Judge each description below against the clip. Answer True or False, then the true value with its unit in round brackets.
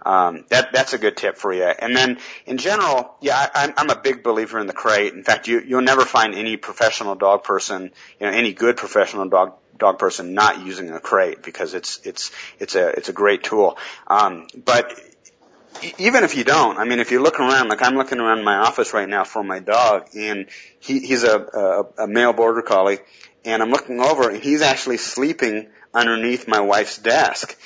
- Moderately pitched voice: False (120 Hz)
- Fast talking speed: True (210 wpm)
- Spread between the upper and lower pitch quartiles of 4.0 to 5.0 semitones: True (4.3 semitones)